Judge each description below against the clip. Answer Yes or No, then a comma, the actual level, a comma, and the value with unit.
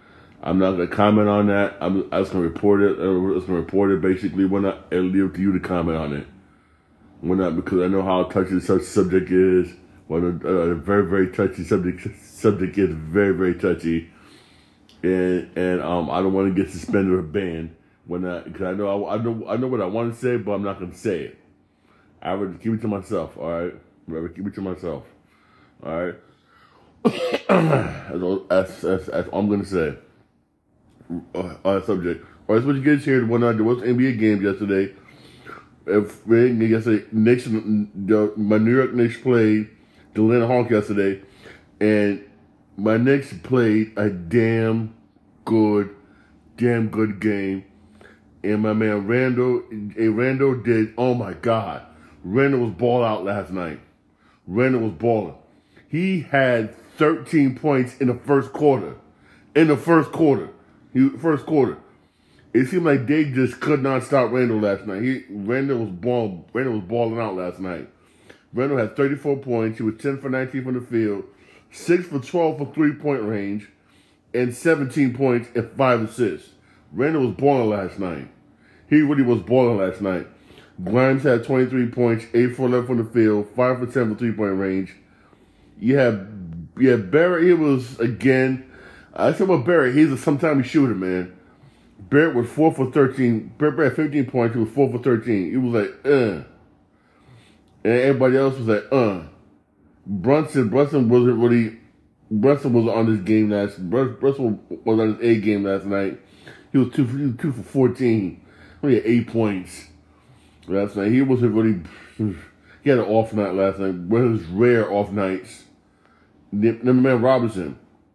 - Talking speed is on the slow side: No, average, 180 wpm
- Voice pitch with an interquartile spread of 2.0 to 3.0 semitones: No, average, 4.6 semitones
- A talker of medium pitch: No, low, 110 Hz